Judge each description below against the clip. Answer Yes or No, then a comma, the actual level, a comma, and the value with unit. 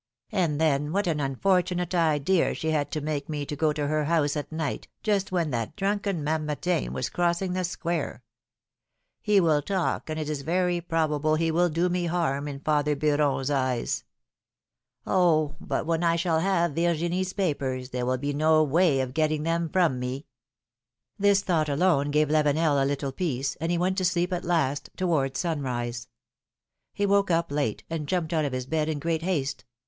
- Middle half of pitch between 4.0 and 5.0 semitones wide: No, average, 3.4 semitones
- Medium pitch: Yes, medium, 155 Hz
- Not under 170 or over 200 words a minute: Yes, average, 185 wpm